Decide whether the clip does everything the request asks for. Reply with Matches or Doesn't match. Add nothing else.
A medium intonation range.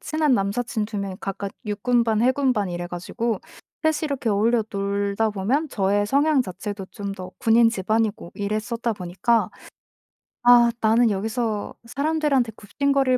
Matches